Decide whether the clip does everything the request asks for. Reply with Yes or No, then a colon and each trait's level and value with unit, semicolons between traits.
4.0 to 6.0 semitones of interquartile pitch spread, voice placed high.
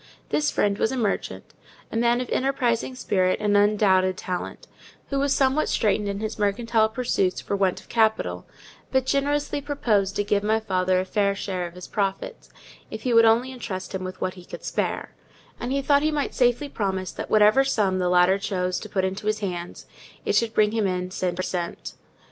Yes: average, 4.5 semitones; high, 210 Hz